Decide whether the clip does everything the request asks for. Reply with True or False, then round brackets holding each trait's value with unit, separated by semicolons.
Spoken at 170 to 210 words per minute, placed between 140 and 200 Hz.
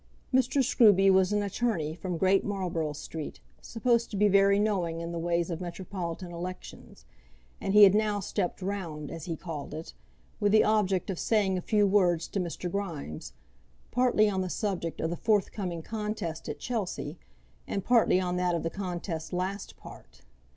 True (175 wpm; 185 Hz)